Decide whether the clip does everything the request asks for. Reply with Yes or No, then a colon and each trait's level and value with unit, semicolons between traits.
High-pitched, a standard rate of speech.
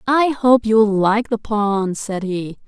Yes: high, 215 Hz; average, 180 wpm